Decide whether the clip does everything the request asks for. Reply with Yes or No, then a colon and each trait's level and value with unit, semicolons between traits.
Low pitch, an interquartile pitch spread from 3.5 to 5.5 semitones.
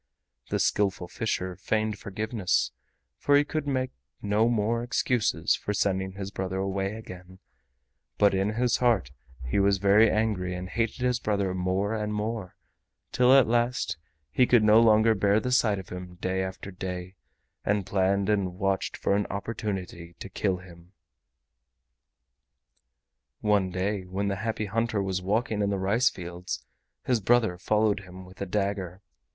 No: low, 100 Hz; average, 2.8 semitones